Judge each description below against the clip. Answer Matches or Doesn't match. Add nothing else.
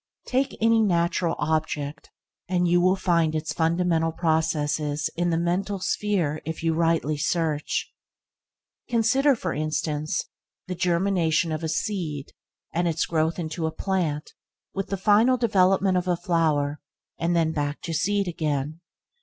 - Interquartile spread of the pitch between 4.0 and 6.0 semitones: Doesn't match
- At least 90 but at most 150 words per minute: Matches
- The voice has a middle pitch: Matches